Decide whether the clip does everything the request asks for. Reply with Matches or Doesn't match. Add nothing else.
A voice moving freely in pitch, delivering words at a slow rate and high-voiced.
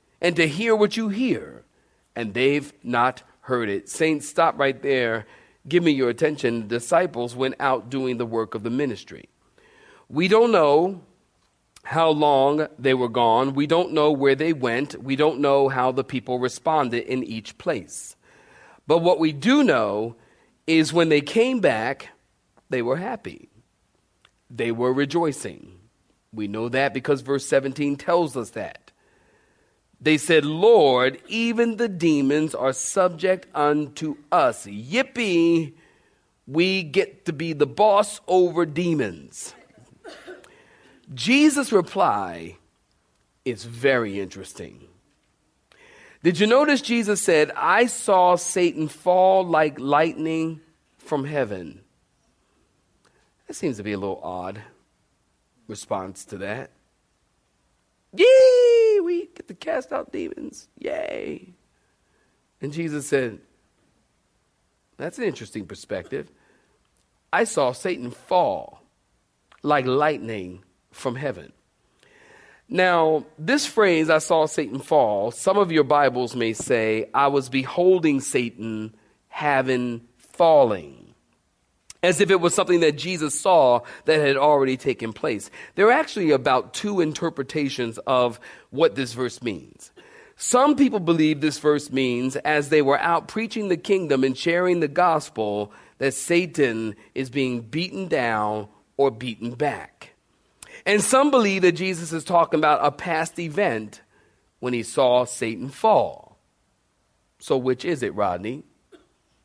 Doesn't match